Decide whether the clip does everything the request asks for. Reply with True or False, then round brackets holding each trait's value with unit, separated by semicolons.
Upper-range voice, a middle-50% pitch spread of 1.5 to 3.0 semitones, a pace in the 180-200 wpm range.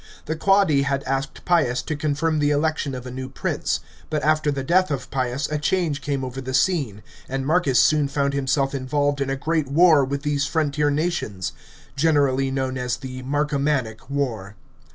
False (140 Hz; 2.5 semitones; 185 wpm)